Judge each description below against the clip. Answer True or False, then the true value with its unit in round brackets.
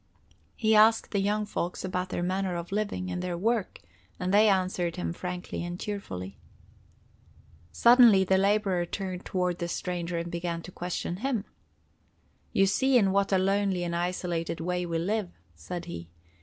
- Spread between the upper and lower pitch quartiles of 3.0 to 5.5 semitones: False (2.4 semitones)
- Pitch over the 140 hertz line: True (185 Hz)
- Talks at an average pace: True (165 wpm)